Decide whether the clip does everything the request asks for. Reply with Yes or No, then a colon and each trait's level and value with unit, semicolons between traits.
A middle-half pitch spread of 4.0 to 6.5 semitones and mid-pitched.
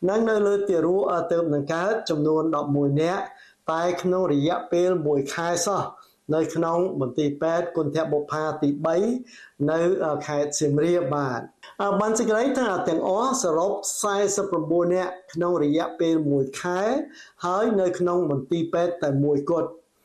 No: average, 3.2 semitones; medium, 170 Hz